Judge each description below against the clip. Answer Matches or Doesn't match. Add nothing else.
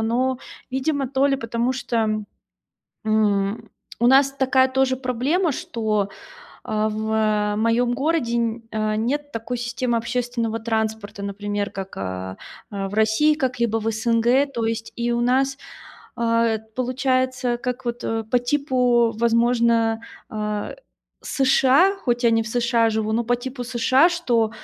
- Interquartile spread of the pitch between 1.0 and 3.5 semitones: Matches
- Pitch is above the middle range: Matches